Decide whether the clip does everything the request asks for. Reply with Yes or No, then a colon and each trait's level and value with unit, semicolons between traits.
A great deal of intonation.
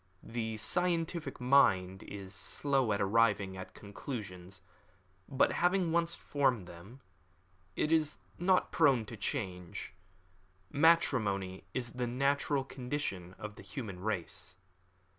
Yes: wide, 6.7 semitones